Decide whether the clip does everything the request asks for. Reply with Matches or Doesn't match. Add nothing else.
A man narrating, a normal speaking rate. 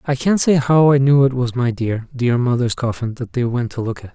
Doesn't match